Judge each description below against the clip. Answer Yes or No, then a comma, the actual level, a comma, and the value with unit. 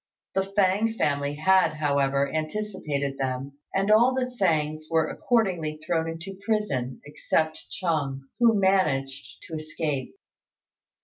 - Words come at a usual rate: No, slow, 120 wpm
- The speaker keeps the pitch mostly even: No, wide, 5.4 semitones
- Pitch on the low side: No, medium, 160 Hz